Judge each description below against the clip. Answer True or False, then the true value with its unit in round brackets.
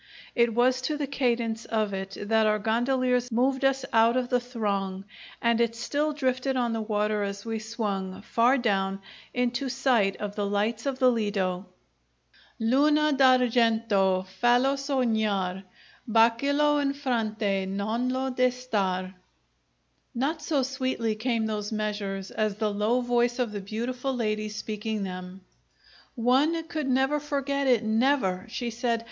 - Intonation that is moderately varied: True (3.5 semitones)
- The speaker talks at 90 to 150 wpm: False (160 wpm)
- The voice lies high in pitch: True (230 Hz)